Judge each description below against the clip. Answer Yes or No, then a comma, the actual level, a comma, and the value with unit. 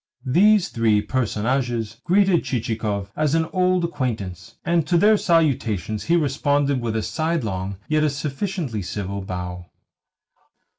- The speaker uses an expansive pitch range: Yes, wide, 7.8 semitones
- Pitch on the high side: No, low, 130 Hz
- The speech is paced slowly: Yes, slow, 130 wpm